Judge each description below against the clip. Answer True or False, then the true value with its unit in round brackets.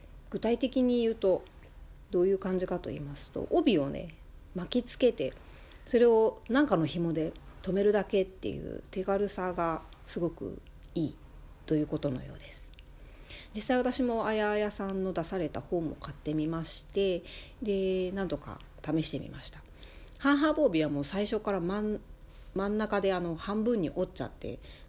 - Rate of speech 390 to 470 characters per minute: False (300 characters per minute)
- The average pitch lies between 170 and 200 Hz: True (185 Hz)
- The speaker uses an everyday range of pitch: False (6.3 semitones)